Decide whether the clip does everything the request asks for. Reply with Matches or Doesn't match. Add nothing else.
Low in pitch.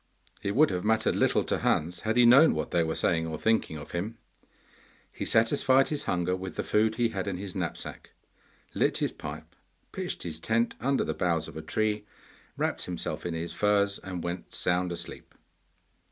Matches